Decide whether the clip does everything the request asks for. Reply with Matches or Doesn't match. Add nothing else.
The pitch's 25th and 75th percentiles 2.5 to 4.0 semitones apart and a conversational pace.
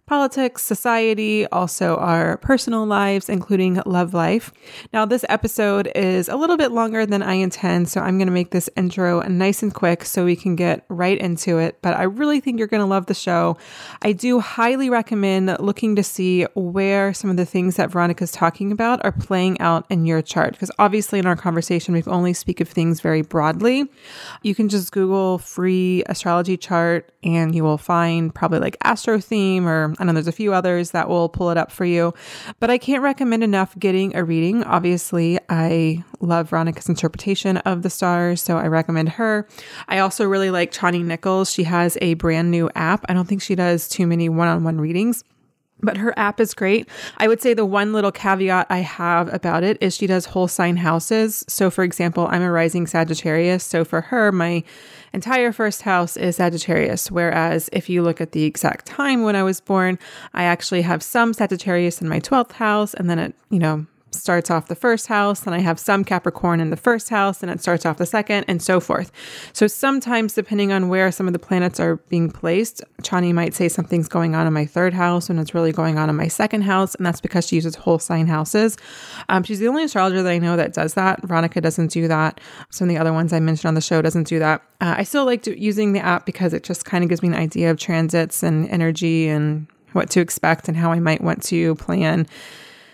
Doesn't match